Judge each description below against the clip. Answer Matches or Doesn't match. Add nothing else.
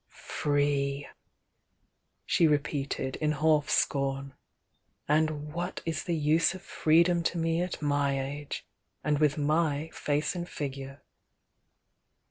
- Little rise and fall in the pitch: Matches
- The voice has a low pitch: Doesn't match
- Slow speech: Matches